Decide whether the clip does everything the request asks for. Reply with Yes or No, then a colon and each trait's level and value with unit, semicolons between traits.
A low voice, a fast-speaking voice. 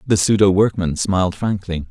No: very low, 95 Hz; average, 160 wpm